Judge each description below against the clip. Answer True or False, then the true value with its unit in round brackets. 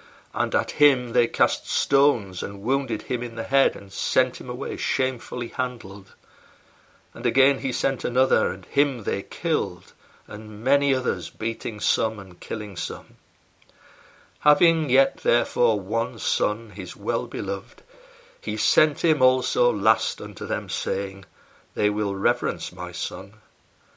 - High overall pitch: False (135 Hz)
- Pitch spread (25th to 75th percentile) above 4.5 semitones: True (5.3 semitones)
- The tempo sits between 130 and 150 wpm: True (140 wpm)